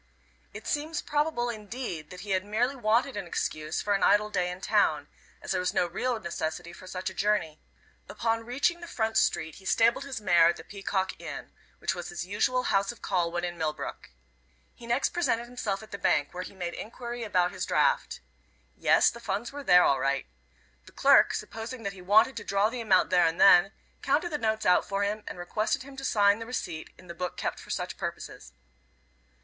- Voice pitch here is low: No, high, 205 Hz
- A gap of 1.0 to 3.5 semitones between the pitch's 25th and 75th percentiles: No, average, 4.8 semitones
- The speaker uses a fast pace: Yes, fast, 210 wpm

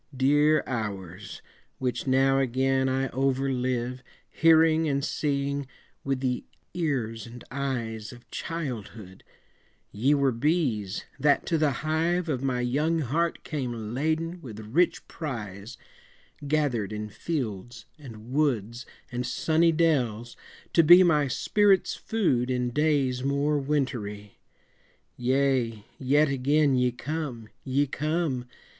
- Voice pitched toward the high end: No, low, 135 Hz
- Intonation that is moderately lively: Yes, average, 4.0 semitones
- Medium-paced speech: No, slow, 120 wpm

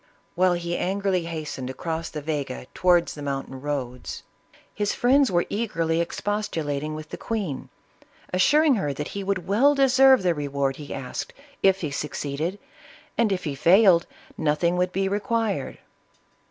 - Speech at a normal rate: Yes, average, 155 wpm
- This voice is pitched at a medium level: Yes, medium, 175 Hz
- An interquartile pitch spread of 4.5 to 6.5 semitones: Yes, average, 5.3 semitones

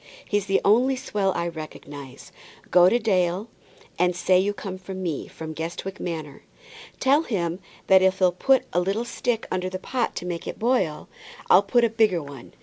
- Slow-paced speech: No, average, 190 wpm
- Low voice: No, medium, 185 Hz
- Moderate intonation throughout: Yes, average, 3.9 semitones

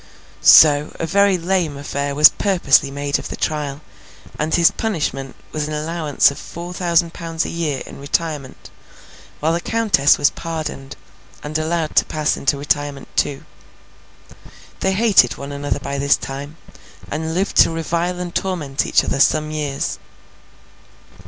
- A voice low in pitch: No, medium, 155 Hz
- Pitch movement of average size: Yes, average, 3.1 semitones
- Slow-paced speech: No, average, 150 wpm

